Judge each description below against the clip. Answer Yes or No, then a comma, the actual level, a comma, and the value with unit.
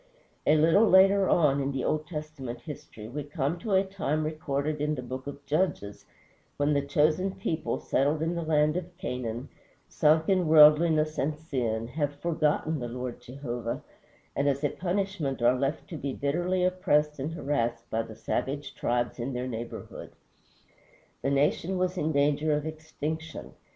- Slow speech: No, average, 165 wpm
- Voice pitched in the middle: Yes, medium, 150 Hz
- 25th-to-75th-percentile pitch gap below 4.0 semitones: Yes, average, 3.1 semitones